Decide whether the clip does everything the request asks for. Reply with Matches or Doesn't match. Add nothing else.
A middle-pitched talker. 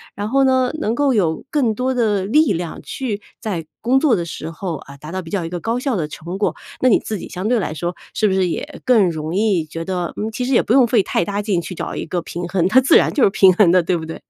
Doesn't match